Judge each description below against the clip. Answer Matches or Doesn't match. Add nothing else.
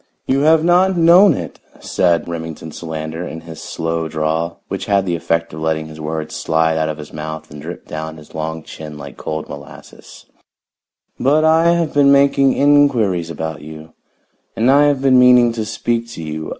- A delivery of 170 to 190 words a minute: Matches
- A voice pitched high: Doesn't match